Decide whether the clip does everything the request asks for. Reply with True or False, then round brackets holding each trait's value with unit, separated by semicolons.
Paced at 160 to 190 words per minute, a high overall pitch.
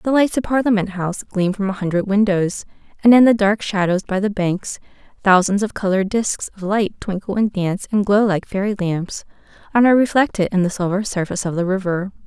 False (205 wpm; 200 Hz)